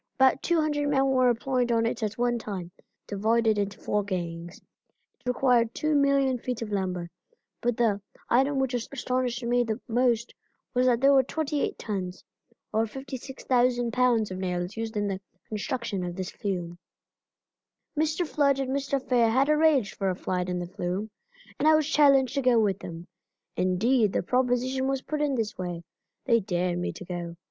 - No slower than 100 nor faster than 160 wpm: No, average, 175 wpm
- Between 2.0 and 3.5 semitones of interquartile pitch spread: No, average, 5.2 semitones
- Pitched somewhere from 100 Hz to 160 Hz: No, high, 235 Hz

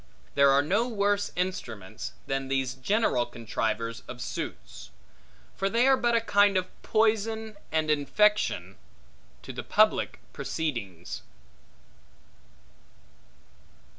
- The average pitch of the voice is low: No, medium, 160 Hz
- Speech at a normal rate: No, slow, 105 wpm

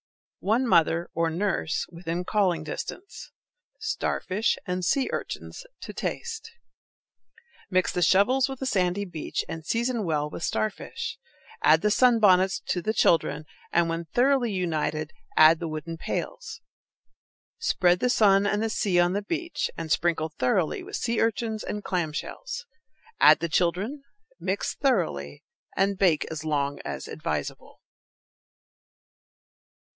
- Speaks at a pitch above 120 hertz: Yes, medium, 185 Hz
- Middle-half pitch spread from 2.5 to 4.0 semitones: No, average, 5.3 semitones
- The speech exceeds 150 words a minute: No, slow, 135 wpm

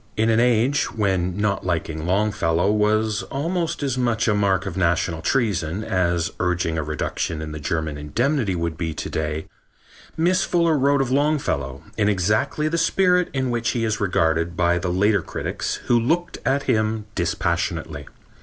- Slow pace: No, average, 165 wpm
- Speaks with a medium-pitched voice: No, low, 105 Hz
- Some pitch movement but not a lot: No, wide, 6.9 semitones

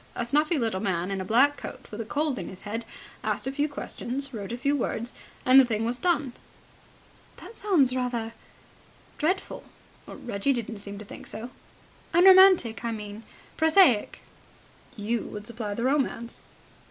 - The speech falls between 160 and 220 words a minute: Yes, average, 165 wpm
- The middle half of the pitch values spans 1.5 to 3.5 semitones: No, average, 4.8 semitones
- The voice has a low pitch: No, high, 240 Hz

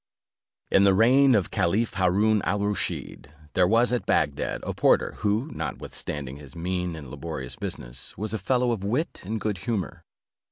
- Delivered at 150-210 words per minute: Yes, average, 165 wpm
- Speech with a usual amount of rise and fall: Yes, average, 4.6 semitones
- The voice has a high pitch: No, low, 100 Hz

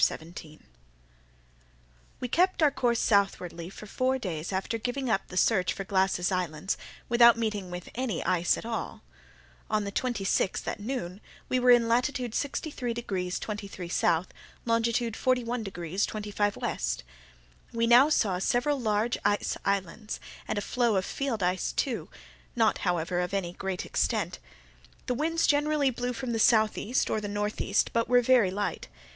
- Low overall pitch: No, high, 215 Hz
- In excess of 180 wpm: No, average, 160 wpm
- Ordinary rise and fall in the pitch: Yes, average, 4.5 semitones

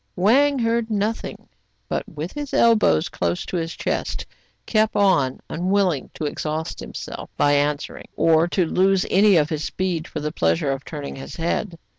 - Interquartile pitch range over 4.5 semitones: Yes, wide, 5.5 semitones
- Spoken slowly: No, average, 165 wpm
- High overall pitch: No, medium, 170 Hz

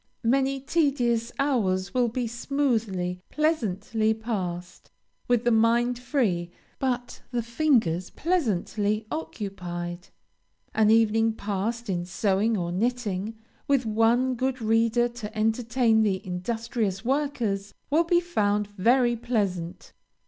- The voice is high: Yes, high, 225 Hz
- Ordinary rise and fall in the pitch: Yes, average, 3.7 semitones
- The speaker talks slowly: Yes, slow, 110 wpm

